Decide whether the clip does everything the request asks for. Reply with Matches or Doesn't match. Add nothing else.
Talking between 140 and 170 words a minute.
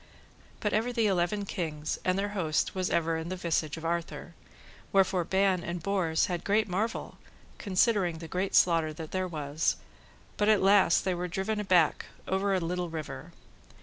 Doesn't match